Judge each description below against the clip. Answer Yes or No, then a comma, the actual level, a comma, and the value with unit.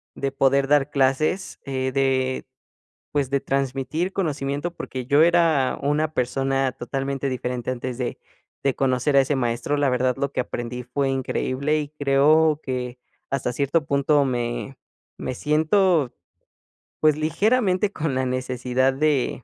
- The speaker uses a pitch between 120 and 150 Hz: Yes, low, 135 Hz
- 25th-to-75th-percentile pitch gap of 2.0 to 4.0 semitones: Yes, average, 2.7 semitones